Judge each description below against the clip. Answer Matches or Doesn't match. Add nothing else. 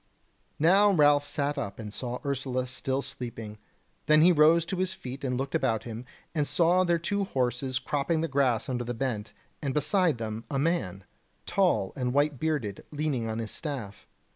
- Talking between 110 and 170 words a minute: Doesn't match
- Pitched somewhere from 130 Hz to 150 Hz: Matches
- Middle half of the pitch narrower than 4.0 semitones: Doesn't match